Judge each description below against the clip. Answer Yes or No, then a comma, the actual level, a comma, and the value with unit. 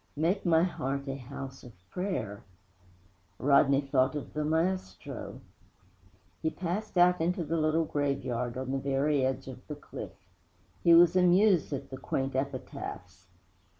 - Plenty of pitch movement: No, average, 4.1 semitones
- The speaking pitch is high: No, medium, 140 Hz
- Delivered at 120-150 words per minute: Yes, average, 145 wpm